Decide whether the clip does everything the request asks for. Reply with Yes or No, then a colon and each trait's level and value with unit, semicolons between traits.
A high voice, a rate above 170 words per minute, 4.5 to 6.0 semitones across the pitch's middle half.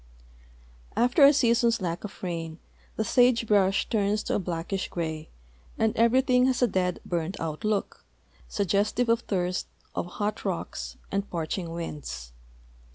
No: high, 200 Hz; average, 145 wpm; average, 5.3 semitones